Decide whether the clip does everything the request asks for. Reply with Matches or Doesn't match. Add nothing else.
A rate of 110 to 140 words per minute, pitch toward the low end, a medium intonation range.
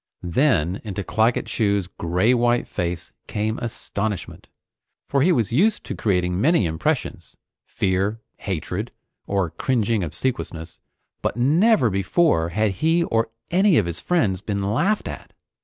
Doesn't match